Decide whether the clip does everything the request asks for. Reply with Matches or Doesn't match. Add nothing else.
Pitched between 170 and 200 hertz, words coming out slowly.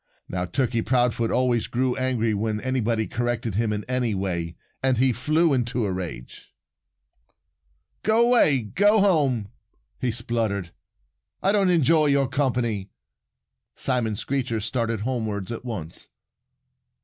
Doesn't match